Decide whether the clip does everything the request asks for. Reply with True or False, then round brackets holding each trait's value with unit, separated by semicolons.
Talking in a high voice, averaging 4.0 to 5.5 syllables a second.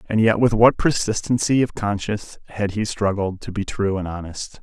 False (105 Hz; 5.1 syllables/s)